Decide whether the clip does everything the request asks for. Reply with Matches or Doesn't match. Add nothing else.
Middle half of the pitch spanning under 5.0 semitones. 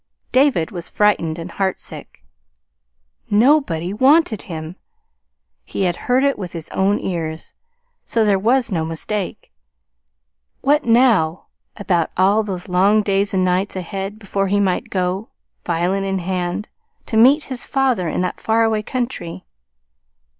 Matches